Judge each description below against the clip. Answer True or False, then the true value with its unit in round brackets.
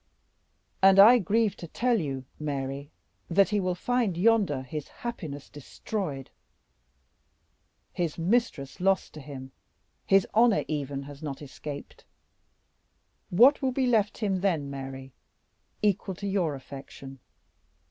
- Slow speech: True (125 wpm)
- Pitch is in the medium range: True (170 Hz)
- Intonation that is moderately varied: False (6.8 semitones)